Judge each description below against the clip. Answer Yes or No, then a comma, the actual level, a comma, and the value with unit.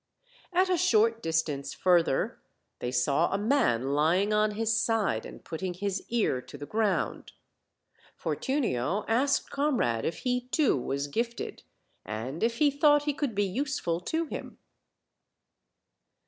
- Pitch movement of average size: No, wide, 8.6 semitones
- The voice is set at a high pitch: Yes, high, 210 Hz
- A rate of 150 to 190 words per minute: No, average, 140 wpm